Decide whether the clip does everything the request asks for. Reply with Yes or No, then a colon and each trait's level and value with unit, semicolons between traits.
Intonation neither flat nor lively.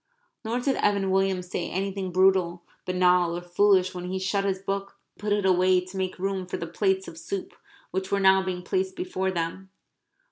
No: narrow, 1.5 semitones